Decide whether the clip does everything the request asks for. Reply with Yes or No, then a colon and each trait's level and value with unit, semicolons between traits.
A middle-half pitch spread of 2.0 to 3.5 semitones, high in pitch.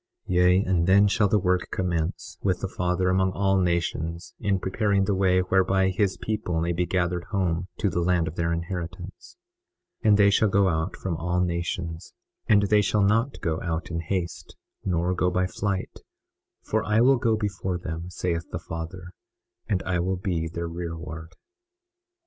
No: narrow, 2.4 semitones; very low, 90 Hz